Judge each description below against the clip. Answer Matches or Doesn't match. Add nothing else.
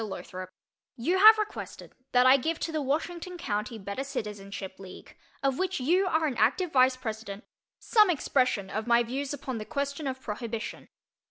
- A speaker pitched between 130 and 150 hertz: Doesn't match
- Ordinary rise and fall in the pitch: Doesn't match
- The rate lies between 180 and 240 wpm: Doesn't match